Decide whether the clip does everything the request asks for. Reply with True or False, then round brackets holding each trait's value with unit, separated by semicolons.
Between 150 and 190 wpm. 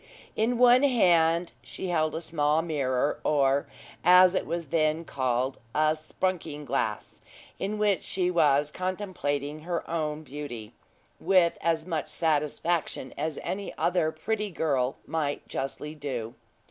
False (135 wpm)